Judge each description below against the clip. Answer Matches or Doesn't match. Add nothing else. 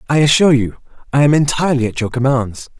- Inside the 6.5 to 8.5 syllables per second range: Matches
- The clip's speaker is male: Matches